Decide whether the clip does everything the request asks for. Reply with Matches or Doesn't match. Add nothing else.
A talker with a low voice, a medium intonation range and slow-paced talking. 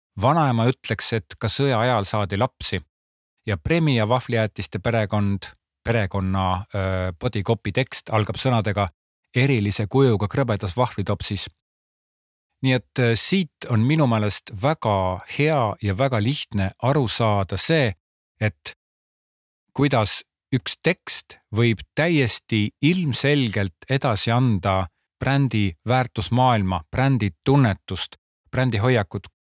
Matches